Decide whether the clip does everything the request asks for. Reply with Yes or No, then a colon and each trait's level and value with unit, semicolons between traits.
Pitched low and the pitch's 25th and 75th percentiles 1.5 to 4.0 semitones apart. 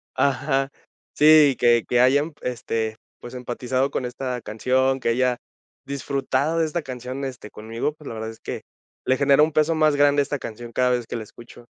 Yes: low, 130 Hz; average, 2.9 semitones